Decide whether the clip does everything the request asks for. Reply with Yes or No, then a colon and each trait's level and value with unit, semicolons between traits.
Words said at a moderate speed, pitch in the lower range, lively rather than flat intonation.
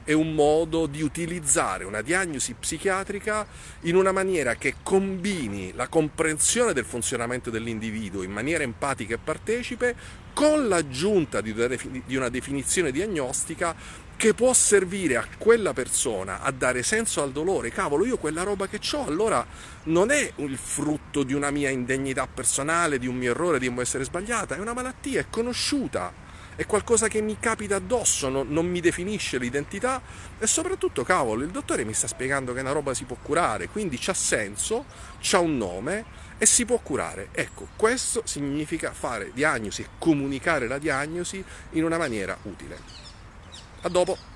No: average, 160 wpm; medium, 165 Hz; wide, 7.6 semitones